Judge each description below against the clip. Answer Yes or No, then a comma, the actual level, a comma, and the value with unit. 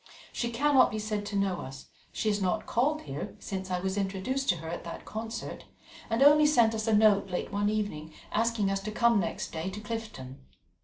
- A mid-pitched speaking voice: No, high, 210 Hz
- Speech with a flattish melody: No, average, 3.3 semitones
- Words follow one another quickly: Yes, fast, 210 wpm